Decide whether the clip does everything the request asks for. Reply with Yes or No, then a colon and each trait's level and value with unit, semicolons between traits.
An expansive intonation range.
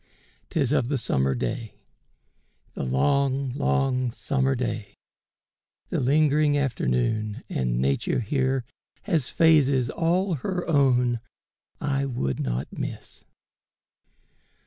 No: average, 4.6 semitones